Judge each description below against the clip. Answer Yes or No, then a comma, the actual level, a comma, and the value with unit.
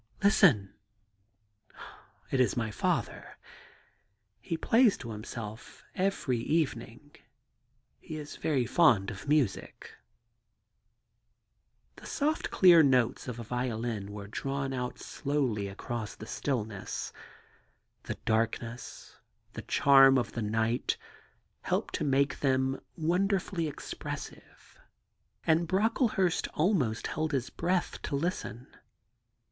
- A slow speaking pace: Yes, slow, 115 wpm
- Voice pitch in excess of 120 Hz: Yes, low, 135 Hz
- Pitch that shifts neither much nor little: No, wide, 5.9 semitones